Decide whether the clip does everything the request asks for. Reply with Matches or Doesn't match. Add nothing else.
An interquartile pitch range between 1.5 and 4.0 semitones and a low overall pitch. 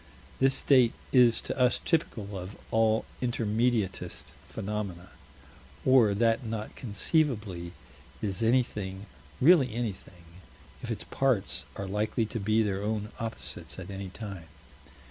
Matches